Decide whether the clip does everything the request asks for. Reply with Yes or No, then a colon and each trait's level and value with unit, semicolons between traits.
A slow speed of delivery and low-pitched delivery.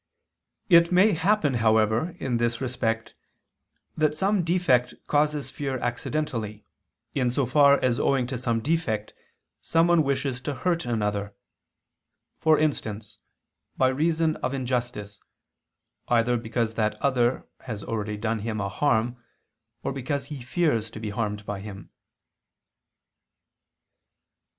Yes: slow, 125 wpm; low, 125 Hz